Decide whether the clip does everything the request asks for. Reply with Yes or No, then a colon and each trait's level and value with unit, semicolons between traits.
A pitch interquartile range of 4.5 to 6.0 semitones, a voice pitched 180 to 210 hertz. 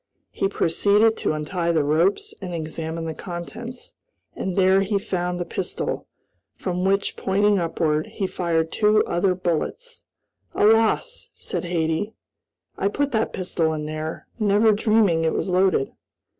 No: average, 4.0 semitones; medium, 185 Hz